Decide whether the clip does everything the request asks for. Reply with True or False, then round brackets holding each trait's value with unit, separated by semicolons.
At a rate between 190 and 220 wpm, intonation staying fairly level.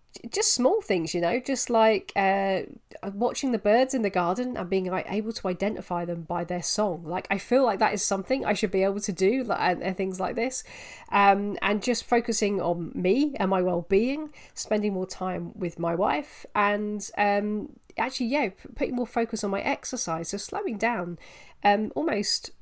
False (195 wpm; 3.9 semitones)